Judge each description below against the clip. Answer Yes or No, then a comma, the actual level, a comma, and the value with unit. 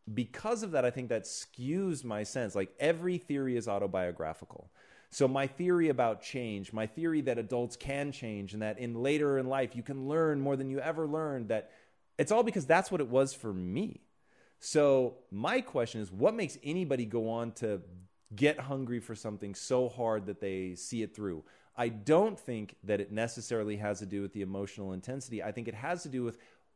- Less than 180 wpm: No, average, 200 wpm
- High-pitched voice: No, low, 120 Hz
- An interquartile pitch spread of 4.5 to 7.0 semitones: Yes, average, 5.0 semitones